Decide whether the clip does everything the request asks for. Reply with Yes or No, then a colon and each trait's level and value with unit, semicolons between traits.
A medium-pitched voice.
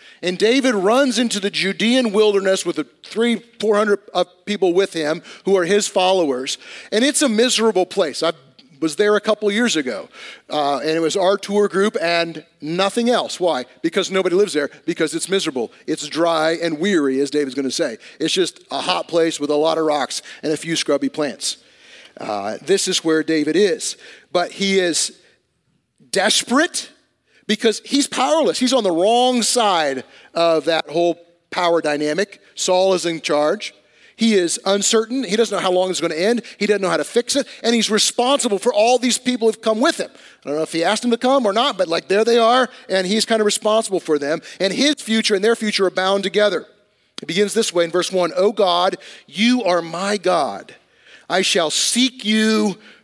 No: high, 195 Hz